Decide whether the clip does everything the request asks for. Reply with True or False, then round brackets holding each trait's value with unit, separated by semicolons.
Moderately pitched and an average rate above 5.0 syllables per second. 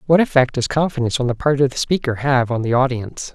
False (130 Hz; 6.6 syllables/s)